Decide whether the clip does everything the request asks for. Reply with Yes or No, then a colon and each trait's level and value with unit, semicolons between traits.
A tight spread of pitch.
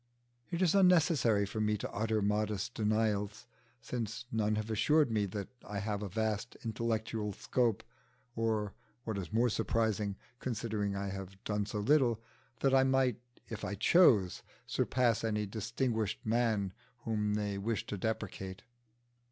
Yes: narrow, 2.1 semitones